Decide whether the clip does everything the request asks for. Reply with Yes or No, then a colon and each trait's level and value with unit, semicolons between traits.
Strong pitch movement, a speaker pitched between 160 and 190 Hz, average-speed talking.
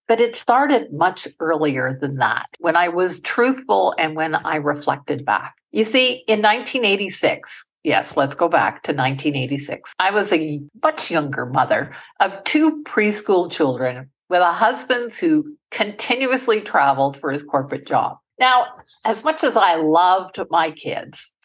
Yes: wide, 7.7 semitones; medium, 185 Hz; average, 150 wpm